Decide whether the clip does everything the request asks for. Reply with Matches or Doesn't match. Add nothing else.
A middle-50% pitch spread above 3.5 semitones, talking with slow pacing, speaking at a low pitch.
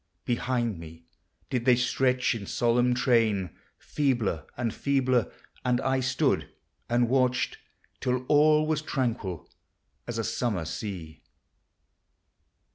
Doesn't match